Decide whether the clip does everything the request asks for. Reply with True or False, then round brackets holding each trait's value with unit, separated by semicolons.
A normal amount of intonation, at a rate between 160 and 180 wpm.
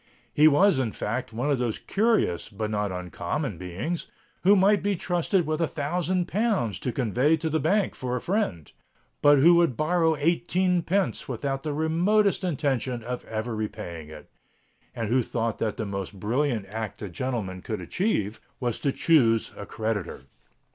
False (7.8 semitones; 170 wpm)